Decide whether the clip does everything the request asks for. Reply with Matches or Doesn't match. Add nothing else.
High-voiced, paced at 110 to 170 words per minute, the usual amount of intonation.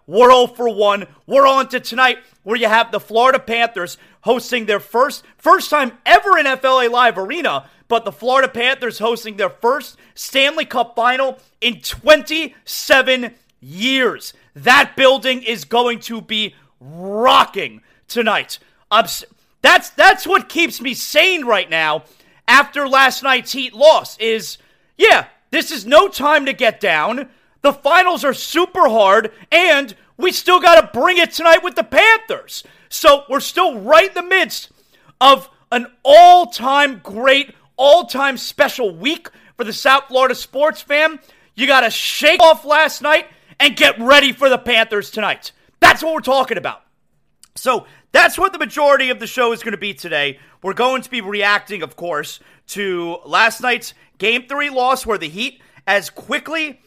Matches